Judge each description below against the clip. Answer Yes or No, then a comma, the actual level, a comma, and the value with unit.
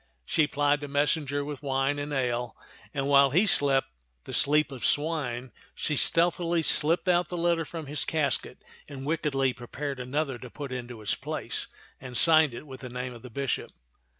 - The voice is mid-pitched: Yes, medium, 145 Hz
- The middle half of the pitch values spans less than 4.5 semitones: Yes, average, 3.0 semitones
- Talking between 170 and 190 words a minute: Yes, average, 180 wpm